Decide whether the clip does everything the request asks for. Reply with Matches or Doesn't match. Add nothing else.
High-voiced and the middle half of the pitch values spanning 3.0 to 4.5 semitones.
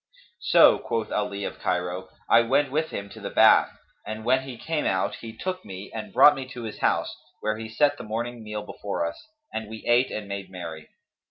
Doesn't match